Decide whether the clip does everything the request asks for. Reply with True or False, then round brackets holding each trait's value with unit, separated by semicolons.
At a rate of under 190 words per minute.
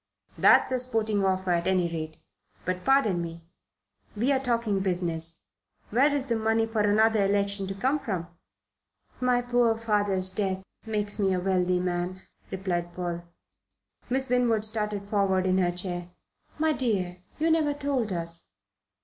True (150 wpm)